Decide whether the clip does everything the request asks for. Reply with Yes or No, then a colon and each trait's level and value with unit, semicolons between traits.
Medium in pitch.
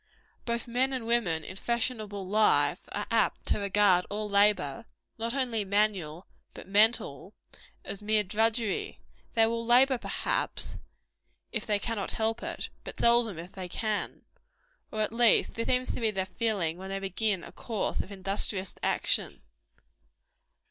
No: high, 215 Hz